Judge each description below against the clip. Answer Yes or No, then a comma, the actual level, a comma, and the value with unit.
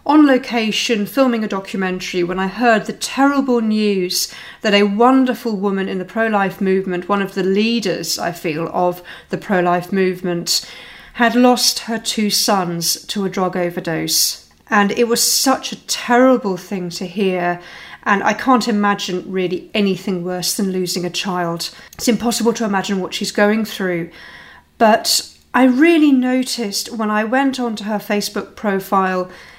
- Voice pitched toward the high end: Yes, high, 200 Hz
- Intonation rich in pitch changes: No, average, 4.3 semitones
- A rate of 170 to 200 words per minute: No, average, 160 wpm